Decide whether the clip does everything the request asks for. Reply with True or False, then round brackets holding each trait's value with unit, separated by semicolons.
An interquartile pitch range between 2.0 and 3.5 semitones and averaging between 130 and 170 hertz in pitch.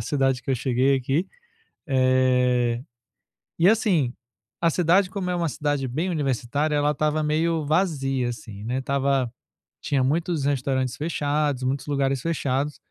True (3.2 semitones; 140 Hz)